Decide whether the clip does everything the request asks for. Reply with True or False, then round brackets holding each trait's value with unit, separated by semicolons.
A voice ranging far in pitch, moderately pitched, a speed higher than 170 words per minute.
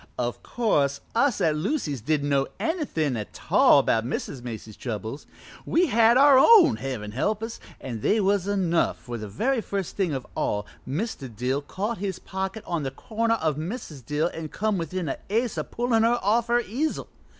True (9.0 semitones; 180 Hz; 185 wpm)